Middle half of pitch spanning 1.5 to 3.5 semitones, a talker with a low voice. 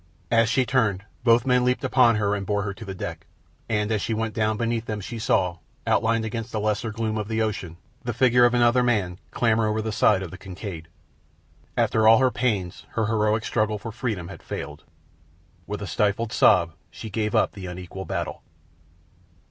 Yes: narrow, 2.5 semitones; low, 110 Hz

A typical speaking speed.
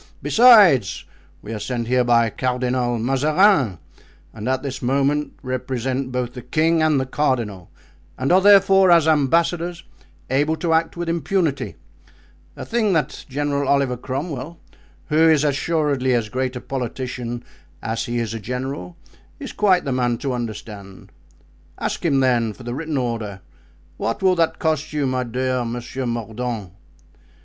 Yes: average, 150 wpm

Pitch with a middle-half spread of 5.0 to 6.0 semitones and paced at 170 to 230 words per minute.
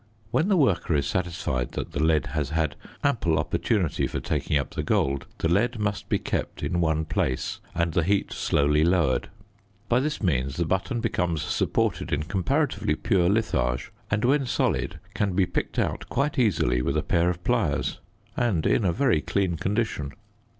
Yes: wide, 5.5 semitones; average, 180 wpm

